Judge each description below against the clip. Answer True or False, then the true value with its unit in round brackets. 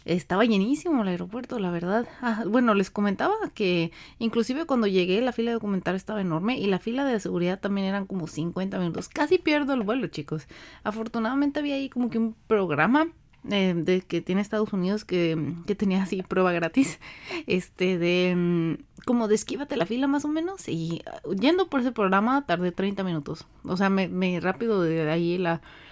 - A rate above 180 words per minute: True (190 wpm)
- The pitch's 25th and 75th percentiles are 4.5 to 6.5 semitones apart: True (5.2 semitones)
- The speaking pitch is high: True (195 Hz)